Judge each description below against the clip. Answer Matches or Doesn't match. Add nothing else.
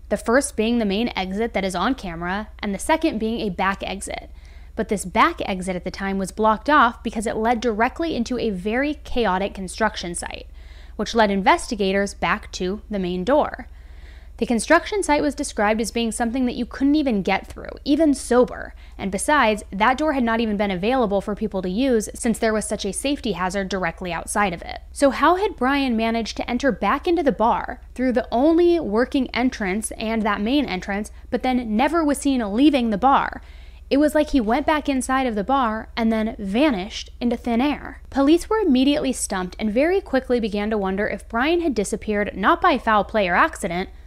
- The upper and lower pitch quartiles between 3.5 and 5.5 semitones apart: Matches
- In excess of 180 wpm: Matches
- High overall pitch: Matches